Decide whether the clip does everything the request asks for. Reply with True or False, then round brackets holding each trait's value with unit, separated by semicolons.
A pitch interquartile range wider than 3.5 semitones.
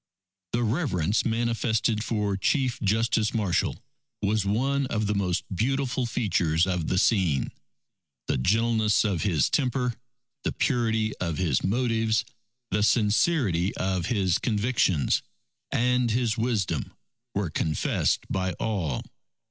True (4.1 semitones)